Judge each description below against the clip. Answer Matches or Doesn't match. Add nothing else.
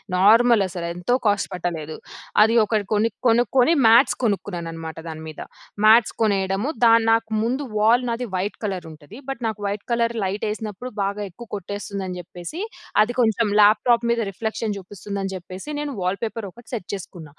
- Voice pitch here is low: Doesn't match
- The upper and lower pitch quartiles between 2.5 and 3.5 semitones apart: Doesn't match